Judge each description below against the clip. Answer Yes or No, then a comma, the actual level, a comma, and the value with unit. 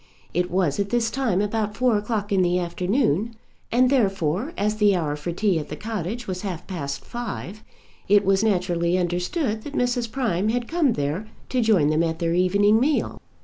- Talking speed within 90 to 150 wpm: No, average, 190 wpm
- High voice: Yes, high, 200 Hz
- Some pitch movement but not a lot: Yes, average, 4.5 semitones